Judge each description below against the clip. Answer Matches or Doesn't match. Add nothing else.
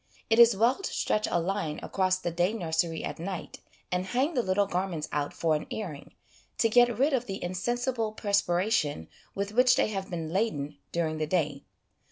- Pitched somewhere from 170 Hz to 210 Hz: Matches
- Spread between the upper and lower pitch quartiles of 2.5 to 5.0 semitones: Doesn't match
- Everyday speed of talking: Matches